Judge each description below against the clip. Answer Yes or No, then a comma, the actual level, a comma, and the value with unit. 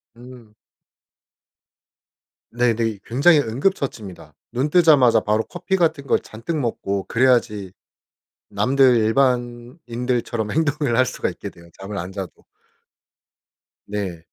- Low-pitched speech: Yes, low, 120 Hz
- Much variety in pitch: No, average, 4.5 semitones